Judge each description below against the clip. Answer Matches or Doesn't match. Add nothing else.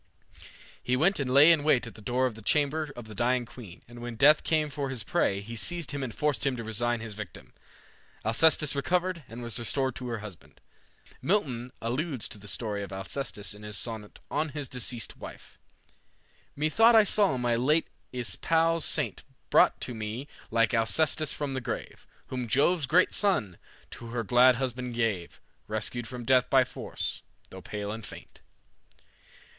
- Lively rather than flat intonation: Doesn't match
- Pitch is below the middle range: Matches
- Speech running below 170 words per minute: Doesn't match